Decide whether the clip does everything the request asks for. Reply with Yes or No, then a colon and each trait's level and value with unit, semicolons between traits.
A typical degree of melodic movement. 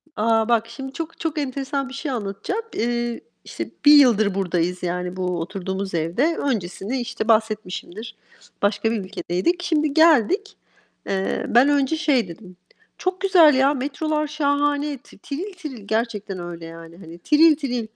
No: wide, 6.9 semitones